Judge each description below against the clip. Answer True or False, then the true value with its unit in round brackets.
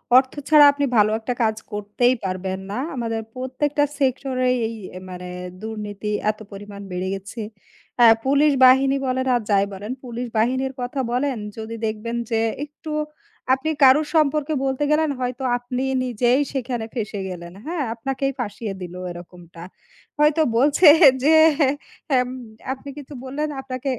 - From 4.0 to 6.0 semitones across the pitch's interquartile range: True (4.3 semitones)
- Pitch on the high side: True (250 Hz)